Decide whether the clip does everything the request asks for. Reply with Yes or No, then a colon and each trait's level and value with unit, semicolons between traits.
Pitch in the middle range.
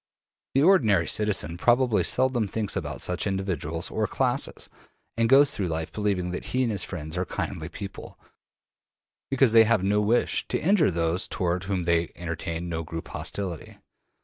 No: very low, 95 Hz